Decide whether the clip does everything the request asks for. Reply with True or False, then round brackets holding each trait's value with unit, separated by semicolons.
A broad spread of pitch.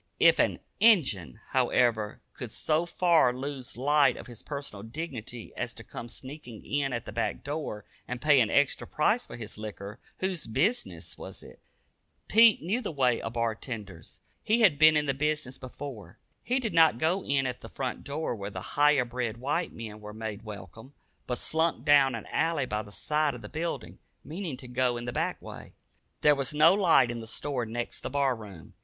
False (4.8 semitones)